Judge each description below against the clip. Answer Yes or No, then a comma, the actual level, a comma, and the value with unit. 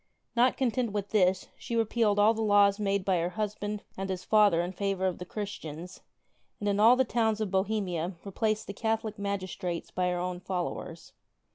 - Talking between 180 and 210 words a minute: Yes, average, 185 wpm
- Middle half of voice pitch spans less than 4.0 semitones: Yes, average, 2.8 semitones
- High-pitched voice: Yes, high, 200 Hz